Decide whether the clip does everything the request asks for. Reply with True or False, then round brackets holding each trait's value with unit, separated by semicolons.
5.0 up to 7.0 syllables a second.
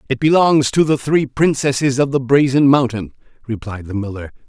True (5.3 syllables/s)